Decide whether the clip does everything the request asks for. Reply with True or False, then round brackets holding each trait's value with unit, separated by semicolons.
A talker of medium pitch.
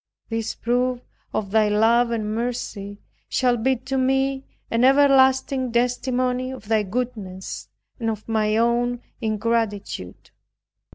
False (235 Hz)